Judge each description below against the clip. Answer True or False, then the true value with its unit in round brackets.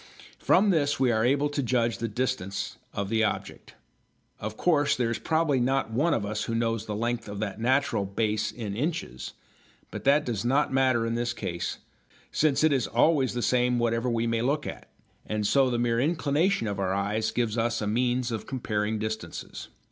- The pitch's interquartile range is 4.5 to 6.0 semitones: False (3.6 semitones)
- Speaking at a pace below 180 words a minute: False (195 wpm)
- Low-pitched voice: True (120 Hz)